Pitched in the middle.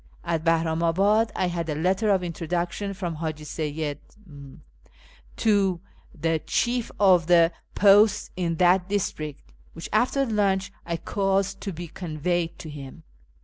Yes: medium, 175 Hz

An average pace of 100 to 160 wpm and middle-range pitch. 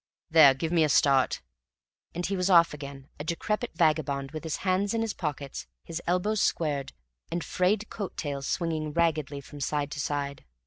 No: average, 180 wpm; medium, 155 Hz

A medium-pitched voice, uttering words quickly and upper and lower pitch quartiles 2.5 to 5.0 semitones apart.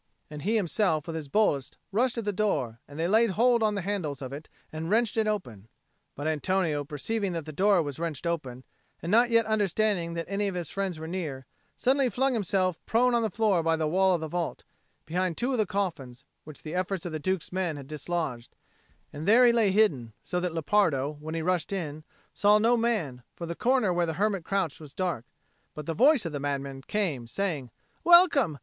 No: medium, 180 Hz; fast, 215 wpm; wide, 5.5 semitones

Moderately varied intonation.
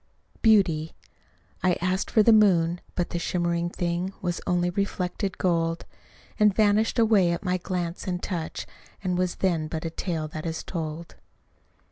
No: narrow, 2.2 semitones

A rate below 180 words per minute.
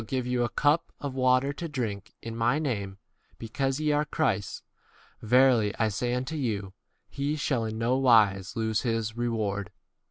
Yes: average, 170 wpm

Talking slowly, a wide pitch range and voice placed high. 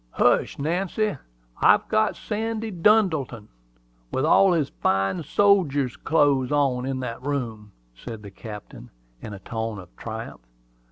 No: slow, 130 wpm; wide, 8.4 semitones; low, 135 Hz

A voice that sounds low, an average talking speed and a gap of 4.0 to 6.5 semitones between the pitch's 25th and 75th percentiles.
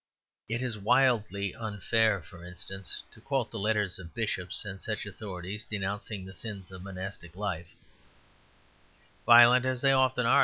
No: low, 105 Hz; average, 150 wpm; average, 3.5 semitones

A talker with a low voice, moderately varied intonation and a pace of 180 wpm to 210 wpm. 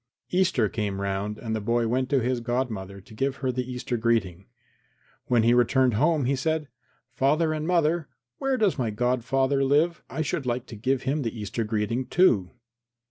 Yes: low, 125 Hz; average, 4.1 semitones; average, 185 wpm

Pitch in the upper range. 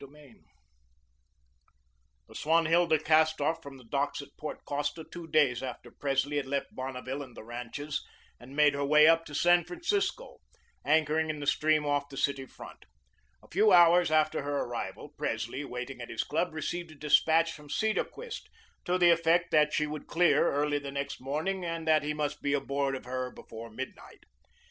No: medium, 150 Hz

